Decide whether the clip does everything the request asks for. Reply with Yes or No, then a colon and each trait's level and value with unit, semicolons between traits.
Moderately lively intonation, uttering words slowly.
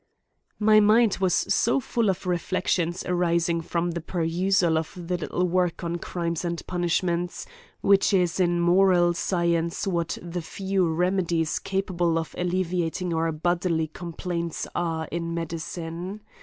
No: narrow, 1.6 semitones; slow, 130 wpm